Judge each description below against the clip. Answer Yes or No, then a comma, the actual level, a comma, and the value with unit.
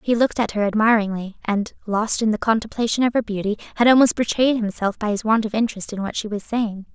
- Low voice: No, high, 220 Hz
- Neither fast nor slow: No, fast, 235 wpm